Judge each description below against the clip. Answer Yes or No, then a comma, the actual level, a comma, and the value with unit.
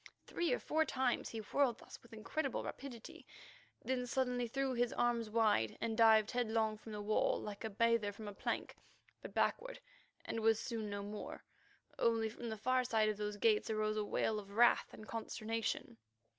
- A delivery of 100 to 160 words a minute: No, average, 185 wpm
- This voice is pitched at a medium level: No, high, 225 Hz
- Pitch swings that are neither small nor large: No, narrow, 2.1 semitones